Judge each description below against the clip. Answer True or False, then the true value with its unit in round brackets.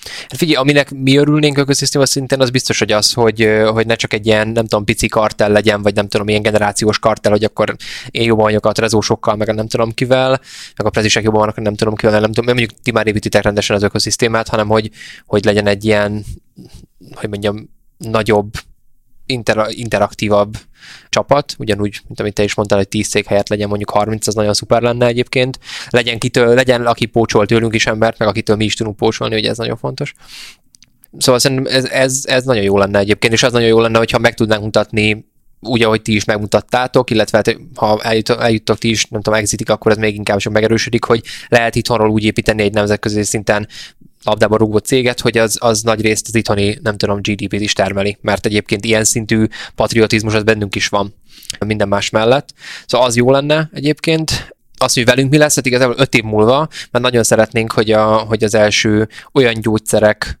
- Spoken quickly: True (200 wpm)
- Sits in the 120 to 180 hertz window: False (110 Hz)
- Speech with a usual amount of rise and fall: False (2.1 semitones)